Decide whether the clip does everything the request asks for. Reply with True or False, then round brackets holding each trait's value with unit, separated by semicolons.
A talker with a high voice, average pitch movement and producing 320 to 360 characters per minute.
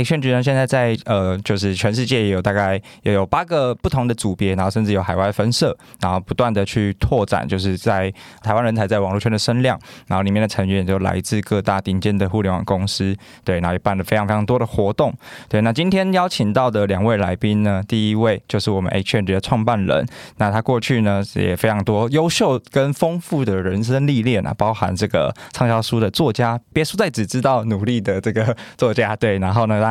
False (110 Hz; 3.6 semitones; 335 characters per minute)